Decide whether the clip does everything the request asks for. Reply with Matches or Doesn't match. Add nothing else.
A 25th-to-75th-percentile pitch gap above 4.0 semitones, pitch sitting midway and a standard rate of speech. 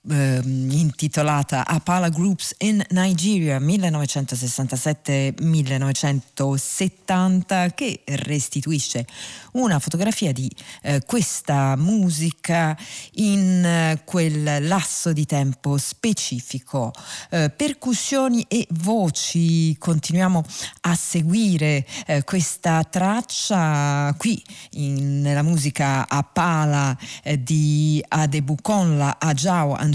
Doesn't match